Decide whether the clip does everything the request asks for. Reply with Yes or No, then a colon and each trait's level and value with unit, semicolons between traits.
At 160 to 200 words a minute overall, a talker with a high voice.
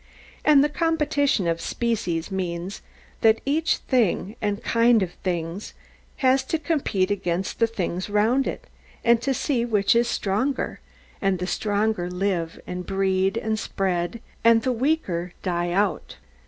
No: average, 150 wpm; high, 205 Hz